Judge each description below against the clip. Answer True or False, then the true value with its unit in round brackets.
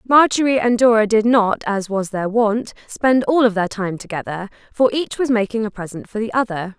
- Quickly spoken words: True (210 wpm)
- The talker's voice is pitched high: True (220 Hz)